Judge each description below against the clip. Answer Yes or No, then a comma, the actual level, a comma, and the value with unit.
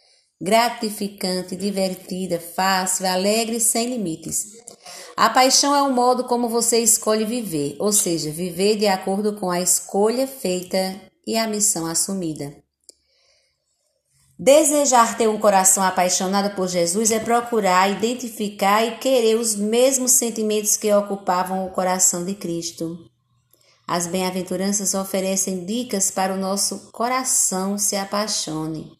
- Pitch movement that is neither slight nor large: Yes, average, 3.5 semitones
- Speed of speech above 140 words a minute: No, average, 125 wpm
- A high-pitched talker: Yes, high, 200 Hz